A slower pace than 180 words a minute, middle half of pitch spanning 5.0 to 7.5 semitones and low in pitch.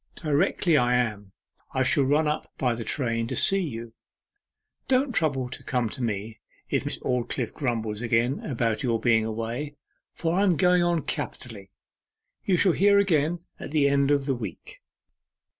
Yes: average, 170 wpm; wide, 5.6 semitones; low, 130 Hz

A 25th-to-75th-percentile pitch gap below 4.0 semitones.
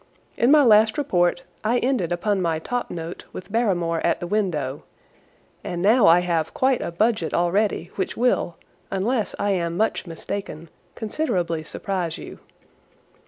No: average, 4.5 semitones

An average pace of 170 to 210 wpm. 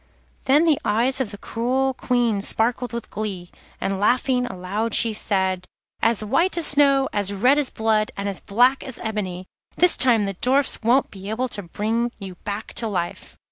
Yes: average, 180 wpm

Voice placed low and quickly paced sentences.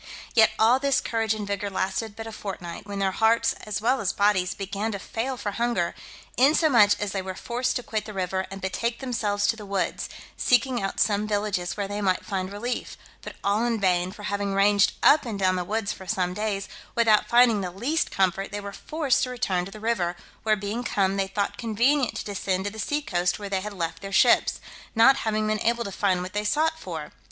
No: high, 205 Hz; fast, 225 wpm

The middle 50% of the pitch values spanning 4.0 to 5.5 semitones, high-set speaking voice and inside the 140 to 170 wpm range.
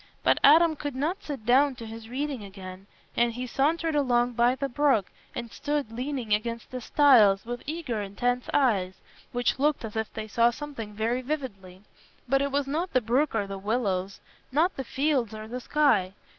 No: average, 4.6 semitones; high, 245 Hz; average, 185 wpm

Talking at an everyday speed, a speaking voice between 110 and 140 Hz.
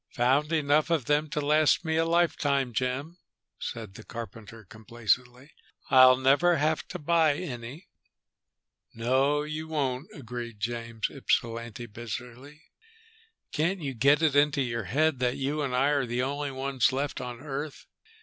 Yes: average, 150 wpm; low, 135 Hz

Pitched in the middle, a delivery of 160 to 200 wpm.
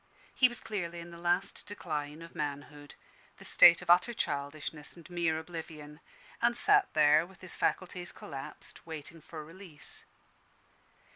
No: medium, 165 Hz; average, 145 wpm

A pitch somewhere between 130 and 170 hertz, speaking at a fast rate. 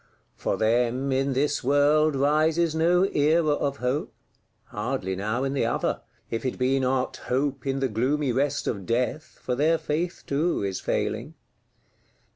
No: low, 135 Hz; average, 150 wpm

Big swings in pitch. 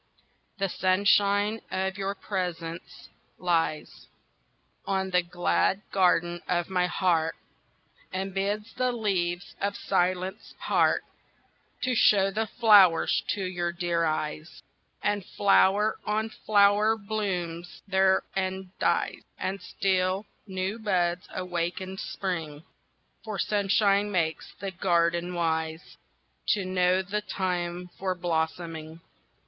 No: narrow, 2.4 semitones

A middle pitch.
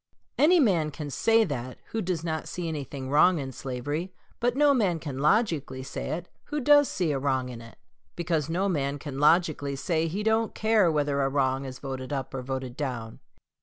Yes: medium, 150 Hz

